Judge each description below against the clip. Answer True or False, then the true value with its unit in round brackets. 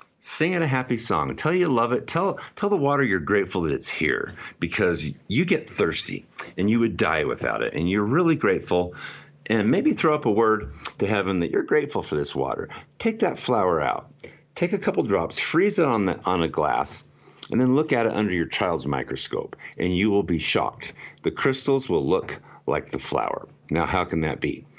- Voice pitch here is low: True (110 Hz)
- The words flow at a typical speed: False (210 wpm)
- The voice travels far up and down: True (7.9 semitones)